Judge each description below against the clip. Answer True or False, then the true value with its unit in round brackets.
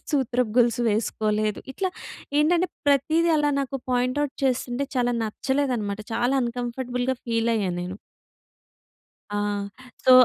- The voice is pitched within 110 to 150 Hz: False (245 Hz)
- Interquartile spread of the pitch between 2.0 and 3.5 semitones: True (3.1 semitones)